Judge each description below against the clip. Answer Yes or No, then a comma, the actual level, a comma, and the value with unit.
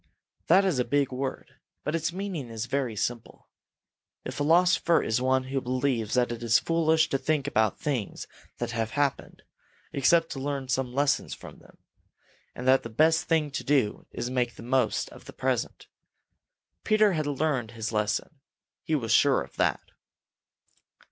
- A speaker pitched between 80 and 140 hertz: Yes, low, 135 Hz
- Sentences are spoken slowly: No, average, 170 wpm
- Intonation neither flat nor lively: Yes, average, 4.5 semitones